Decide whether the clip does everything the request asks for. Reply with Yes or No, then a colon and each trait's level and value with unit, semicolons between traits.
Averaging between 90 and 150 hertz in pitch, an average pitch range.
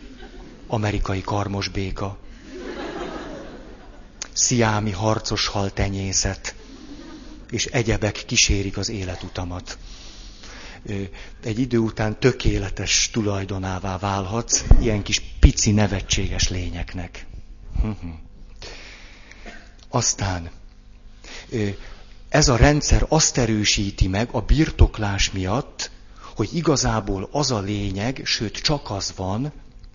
Yes: low, 105 Hz; average, 3.3 semitones